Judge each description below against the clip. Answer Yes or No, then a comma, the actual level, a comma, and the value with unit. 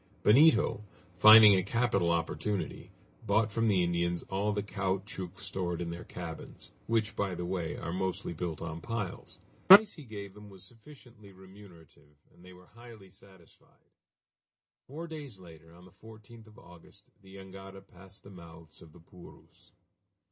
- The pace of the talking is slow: No, average, 160 wpm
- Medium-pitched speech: No, very low, 95 Hz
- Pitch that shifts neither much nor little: Yes, average, 3.6 semitones